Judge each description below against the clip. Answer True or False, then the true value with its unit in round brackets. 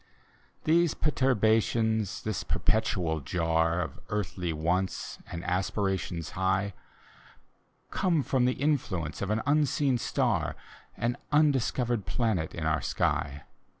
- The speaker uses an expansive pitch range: True (6.4 semitones)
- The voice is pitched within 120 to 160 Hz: False (105 Hz)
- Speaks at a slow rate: True (110 wpm)